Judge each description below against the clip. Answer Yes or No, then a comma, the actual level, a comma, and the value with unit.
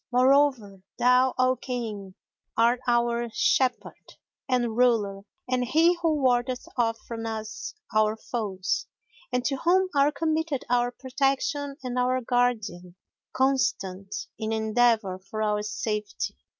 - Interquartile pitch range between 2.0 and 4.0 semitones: Yes, average, 3.2 semitones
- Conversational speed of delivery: No, slow, 125 wpm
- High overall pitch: Yes, high, 245 Hz